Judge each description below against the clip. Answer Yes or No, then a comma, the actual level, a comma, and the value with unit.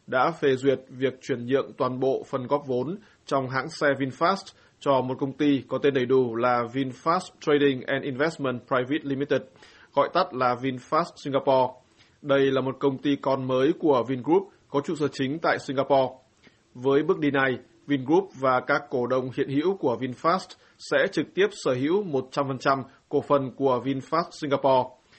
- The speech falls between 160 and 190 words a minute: Yes, average, 175 wpm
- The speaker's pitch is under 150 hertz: Yes, low, 135 Hz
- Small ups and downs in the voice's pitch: Yes, narrow, 1.9 semitones